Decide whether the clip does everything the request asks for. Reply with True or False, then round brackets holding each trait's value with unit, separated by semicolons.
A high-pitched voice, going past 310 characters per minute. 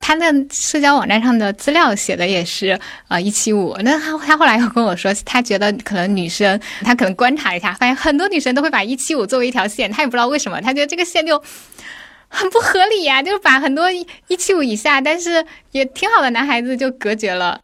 True (265 Hz; 345 characters per minute)